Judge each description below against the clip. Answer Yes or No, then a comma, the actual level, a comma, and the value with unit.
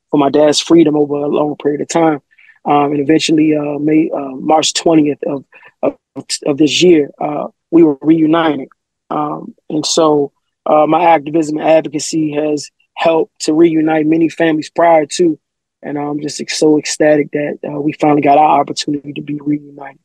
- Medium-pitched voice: Yes, medium, 150 Hz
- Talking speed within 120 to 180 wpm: Yes, average, 175 wpm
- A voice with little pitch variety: Yes, narrow, 1.4 semitones